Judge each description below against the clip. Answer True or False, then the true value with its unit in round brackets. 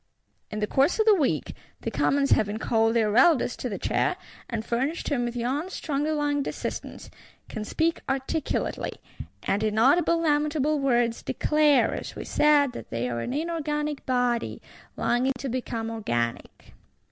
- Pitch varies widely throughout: False (4.6 semitones)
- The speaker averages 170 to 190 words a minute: False (155 wpm)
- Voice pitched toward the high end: True (265 Hz)